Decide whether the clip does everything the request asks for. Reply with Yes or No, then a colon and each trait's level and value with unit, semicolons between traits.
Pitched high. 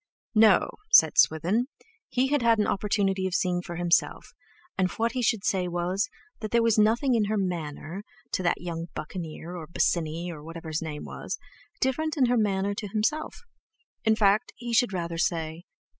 Yes: high, 195 Hz